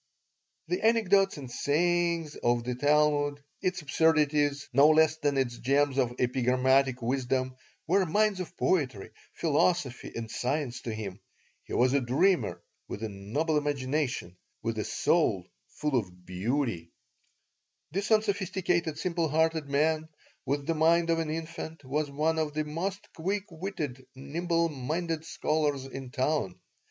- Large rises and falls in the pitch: No, average, 4.2 semitones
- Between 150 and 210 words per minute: No, average, 140 wpm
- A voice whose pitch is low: No, medium, 150 Hz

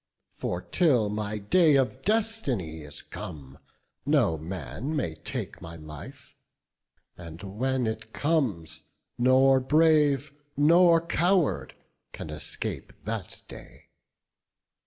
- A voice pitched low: Yes, low, 120 Hz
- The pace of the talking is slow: Yes, slow, 105 wpm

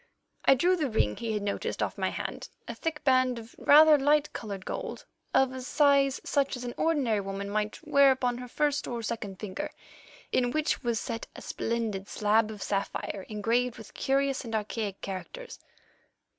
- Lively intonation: No, average, 4.6 semitones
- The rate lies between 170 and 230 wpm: Yes, average, 180 wpm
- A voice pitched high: Yes, high, 240 Hz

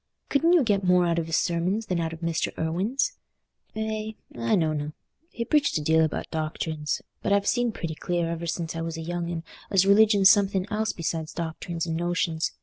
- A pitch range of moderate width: Yes, average, 3.9 semitones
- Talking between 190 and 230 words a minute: Yes, average, 200 wpm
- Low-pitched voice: No, medium, 170 Hz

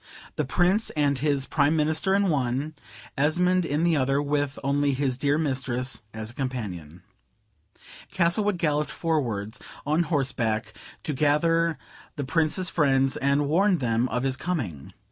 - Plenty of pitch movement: No, average, 3.9 semitones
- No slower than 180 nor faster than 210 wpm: No, average, 145 wpm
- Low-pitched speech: No, medium, 145 Hz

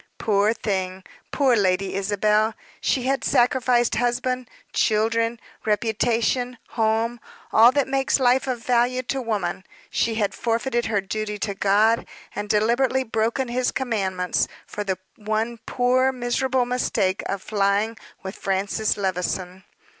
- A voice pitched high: Yes, high, 225 Hz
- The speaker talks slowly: Yes, slow, 130 wpm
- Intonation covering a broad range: No, average, 3.3 semitones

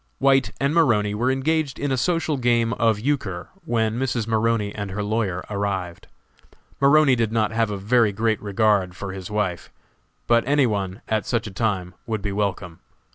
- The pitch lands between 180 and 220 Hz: No, low, 110 Hz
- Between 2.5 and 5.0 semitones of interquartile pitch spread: Yes, average, 3.6 semitones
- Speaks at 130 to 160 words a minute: No, average, 180 wpm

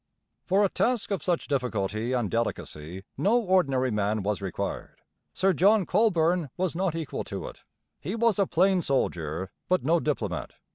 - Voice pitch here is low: No, medium, 160 Hz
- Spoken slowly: No, average, 160 wpm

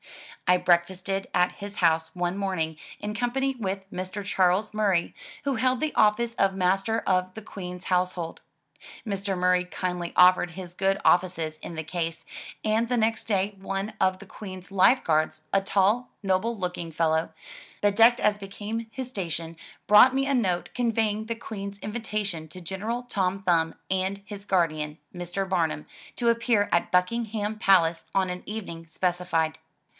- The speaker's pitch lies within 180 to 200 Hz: Yes, high, 190 Hz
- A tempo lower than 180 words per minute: Yes, average, 160 wpm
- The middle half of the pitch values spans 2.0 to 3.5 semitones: Yes, average, 3.1 semitones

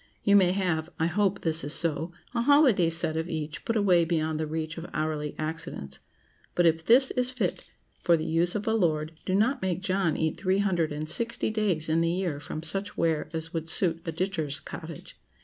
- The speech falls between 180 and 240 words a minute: Yes, average, 200 wpm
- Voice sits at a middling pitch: Yes, medium, 170 Hz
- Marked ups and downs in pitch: No, average, 3.5 semitones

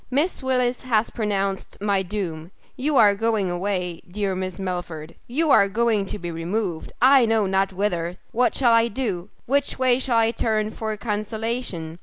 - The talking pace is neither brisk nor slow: Yes, average, 170 wpm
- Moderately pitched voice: No, high, 210 Hz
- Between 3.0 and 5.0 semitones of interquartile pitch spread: Yes, average, 4.1 semitones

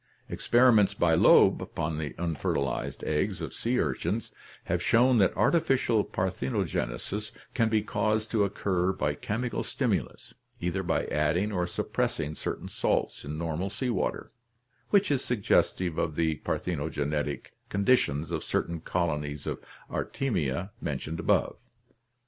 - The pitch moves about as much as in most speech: No, wide, 5.9 semitones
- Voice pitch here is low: Yes, very low, 90 Hz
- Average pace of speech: No, slow, 130 wpm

